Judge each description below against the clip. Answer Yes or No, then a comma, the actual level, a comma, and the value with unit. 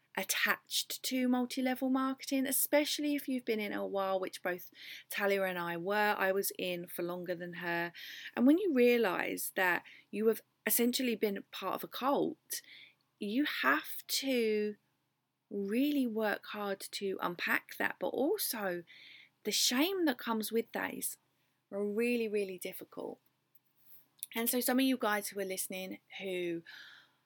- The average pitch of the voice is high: Yes, high, 215 Hz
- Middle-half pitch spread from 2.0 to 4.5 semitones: No, average, 5.0 semitones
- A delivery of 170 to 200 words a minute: No, average, 150 wpm